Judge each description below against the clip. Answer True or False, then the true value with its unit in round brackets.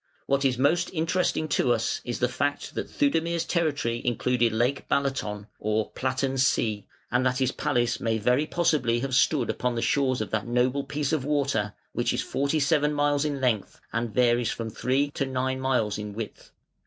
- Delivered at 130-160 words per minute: False (185 wpm)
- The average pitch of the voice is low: True (130 Hz)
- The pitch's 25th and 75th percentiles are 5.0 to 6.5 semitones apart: False (3.2 semitones)